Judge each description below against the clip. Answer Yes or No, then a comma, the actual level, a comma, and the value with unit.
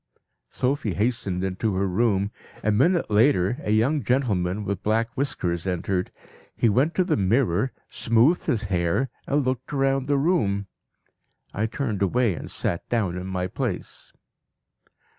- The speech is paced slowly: No, average, 145 wpm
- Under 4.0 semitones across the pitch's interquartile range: No, wide, 5.6 semitones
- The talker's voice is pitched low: Yes, low, 110 Hz